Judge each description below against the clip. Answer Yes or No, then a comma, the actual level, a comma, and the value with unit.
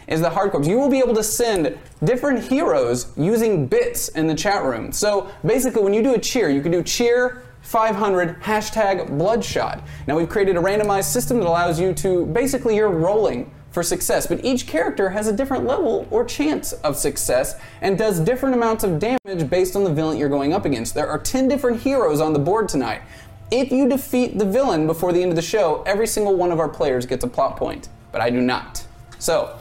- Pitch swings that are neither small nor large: No, wide, 6.8 semitones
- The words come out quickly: Yes, fast, 215 wpm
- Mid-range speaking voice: No, high, 200 Hz